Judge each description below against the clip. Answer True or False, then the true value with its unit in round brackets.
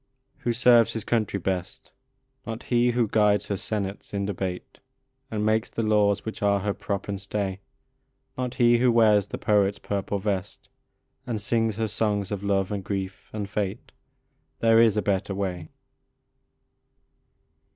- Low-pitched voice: True (105 Hz)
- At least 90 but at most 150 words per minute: False (160 wpm)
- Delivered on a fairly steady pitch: True (2.2 semitones)